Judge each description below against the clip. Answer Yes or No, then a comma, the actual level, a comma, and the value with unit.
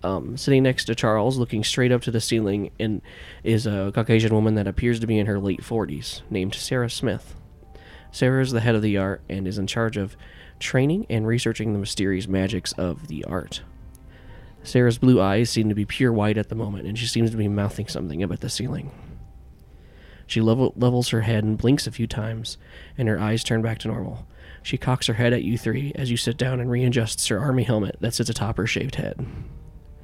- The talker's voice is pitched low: Yes, low, 110 Hz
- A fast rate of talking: Yes, fast, 215 wpm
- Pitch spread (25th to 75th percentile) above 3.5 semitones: No, average, 3.2 semitones